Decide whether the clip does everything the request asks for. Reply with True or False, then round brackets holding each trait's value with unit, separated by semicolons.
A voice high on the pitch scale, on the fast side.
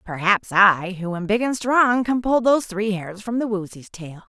True (210 Hz; 235 wpm)